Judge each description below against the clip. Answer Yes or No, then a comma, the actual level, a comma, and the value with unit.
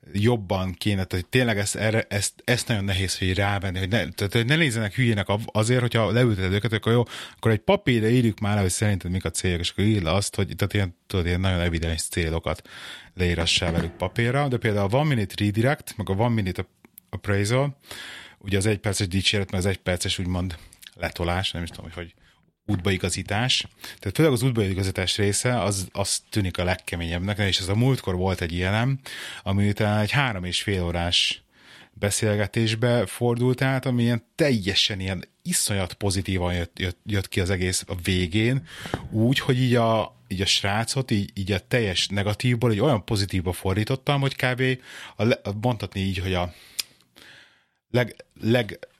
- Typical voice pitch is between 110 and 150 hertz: No, low, 100 Hz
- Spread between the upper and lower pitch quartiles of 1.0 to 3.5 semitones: No, average, 4.0 semitones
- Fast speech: Yes, fast, 175 wpm